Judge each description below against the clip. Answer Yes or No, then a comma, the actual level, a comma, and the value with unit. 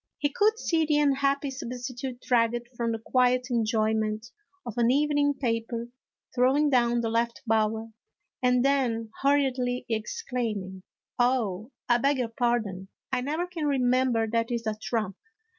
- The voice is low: No, high, 245 Hz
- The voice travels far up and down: No, average, 3.0 semitones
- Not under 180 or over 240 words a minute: No, average, 145 wpm